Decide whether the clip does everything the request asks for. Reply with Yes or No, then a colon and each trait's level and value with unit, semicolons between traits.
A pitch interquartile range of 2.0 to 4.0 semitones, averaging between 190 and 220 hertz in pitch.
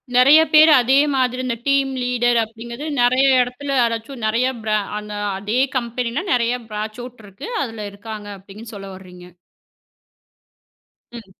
No: average, 3.1 semitones; high, 235 Hz